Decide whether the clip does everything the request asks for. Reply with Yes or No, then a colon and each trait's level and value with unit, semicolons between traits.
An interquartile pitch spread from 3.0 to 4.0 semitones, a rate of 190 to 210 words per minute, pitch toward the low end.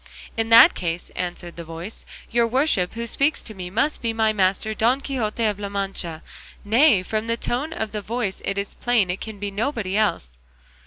No: average, 3.5 semitones; average, 200 wpm; high, 215 Hz